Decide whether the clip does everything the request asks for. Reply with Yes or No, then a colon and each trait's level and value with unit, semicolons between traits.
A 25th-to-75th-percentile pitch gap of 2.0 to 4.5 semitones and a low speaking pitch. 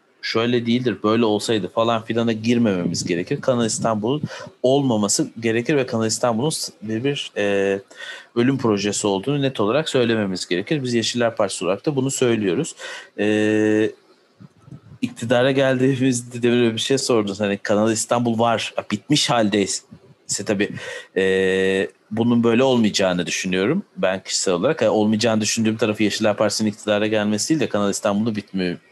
Yes: narrow, 2.6 semitones; low, 115 Hz